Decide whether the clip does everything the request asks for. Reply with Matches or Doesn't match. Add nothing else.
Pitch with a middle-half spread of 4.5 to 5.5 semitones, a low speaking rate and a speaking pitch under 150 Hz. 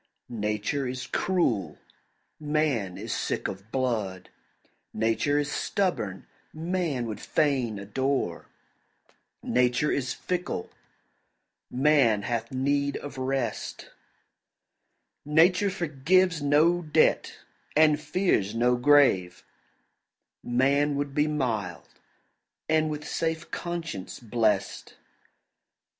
Matches